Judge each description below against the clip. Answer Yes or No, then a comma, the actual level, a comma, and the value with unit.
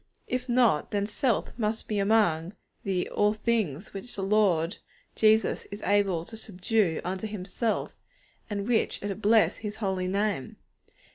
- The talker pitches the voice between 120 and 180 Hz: No, high, 205 Hz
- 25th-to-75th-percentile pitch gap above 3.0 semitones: No, narrow, 2.6 semitones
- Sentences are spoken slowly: No, average, 155 wpm